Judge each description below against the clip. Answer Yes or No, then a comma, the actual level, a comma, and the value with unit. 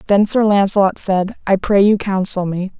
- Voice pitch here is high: Yes, high, 195 Hz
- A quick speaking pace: No, average, 195 wpm